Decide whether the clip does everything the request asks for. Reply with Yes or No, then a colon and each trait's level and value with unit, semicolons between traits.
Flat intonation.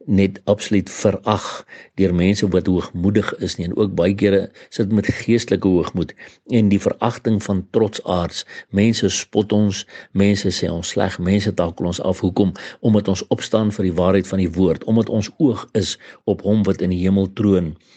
Yes: narrow, 2.3 semitones